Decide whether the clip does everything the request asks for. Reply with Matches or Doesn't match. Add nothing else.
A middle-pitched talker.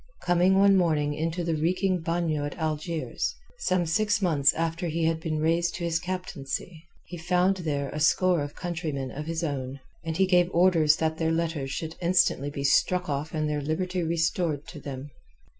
Matches